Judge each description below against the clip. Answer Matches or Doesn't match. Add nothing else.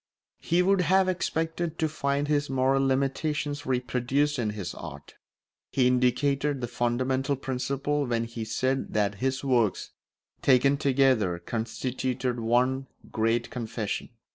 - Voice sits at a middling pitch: Doesn't match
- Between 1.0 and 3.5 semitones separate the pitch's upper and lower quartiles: Matches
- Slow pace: Matches